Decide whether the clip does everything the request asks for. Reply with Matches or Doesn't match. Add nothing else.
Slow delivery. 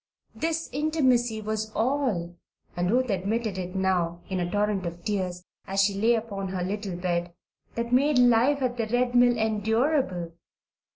Doesn't match